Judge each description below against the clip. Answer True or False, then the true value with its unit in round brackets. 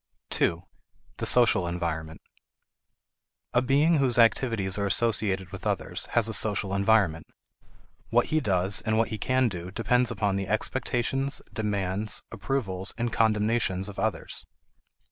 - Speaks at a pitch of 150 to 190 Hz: False (105 Hz)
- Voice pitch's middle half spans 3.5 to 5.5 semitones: True (3.9 semitones)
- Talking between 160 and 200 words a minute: False (135 wpm)